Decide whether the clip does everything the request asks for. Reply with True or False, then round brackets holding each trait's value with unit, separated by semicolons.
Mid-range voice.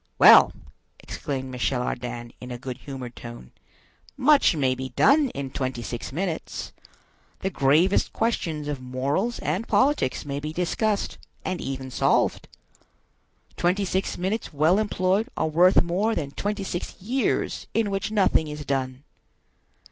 True (155 Hz)